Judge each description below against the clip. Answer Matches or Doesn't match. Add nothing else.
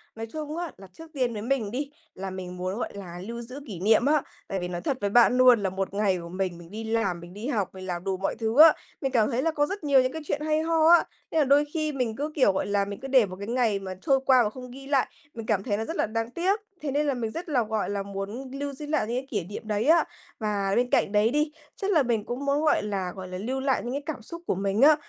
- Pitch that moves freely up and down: Matches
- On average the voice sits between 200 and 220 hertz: Doesn't match